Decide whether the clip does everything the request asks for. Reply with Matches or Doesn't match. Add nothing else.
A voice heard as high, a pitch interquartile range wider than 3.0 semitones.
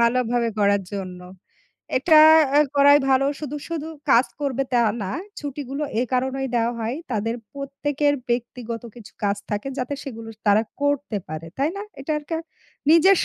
Matches